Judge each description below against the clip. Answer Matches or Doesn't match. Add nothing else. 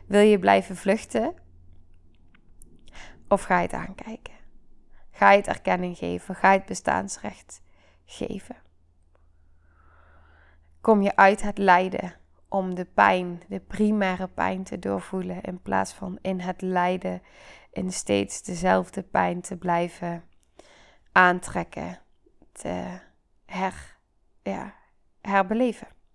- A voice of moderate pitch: Matches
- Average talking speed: Doesn't match